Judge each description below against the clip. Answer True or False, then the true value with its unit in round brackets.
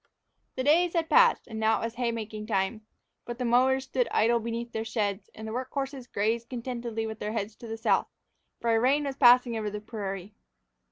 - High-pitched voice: True (230 Hz)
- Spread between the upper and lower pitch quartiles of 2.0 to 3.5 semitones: True (2.5 semitones)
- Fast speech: True (210 wpm)